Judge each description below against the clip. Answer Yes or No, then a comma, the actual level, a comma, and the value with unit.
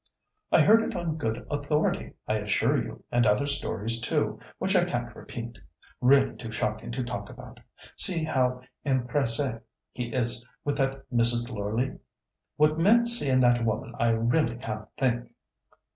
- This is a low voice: Yes, low, 125 Hz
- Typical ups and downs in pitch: Yes, average, 3.8 semitones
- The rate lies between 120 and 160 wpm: Yes, average, 155 wpm